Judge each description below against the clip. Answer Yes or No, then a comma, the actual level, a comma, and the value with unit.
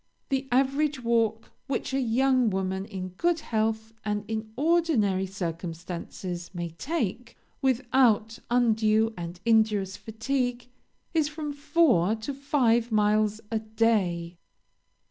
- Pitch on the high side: Yes, high, 225 Hz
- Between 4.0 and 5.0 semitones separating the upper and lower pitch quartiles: Yes, average, 4.7 semitones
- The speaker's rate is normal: No, slow, 115 wpm